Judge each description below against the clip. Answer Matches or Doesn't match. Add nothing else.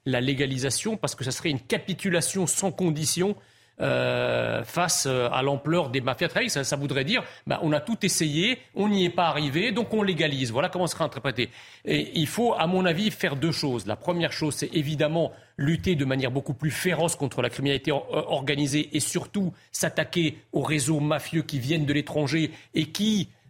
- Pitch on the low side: Doesn't match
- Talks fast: Doesn't match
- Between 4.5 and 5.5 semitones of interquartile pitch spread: Doesn't match